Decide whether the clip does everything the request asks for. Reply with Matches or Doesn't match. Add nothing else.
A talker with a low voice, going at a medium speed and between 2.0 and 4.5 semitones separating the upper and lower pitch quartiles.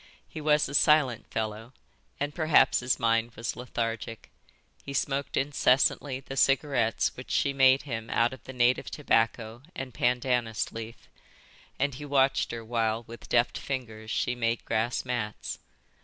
Matches